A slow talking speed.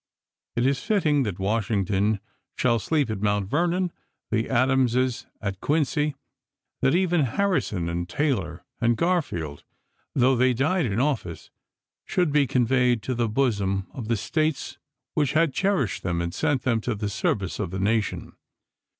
No: average, 155 wpm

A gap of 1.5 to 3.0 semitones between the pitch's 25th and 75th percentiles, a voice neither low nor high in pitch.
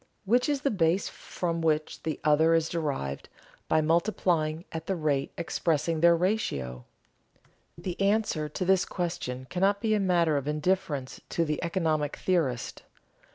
No: average, 3.5 semitones; medium, 165 Hz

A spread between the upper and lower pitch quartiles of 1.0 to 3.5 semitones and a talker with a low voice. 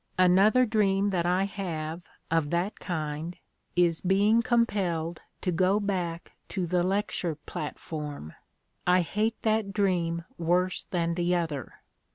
No: average, 3.0 semitones; medium, 180 Hz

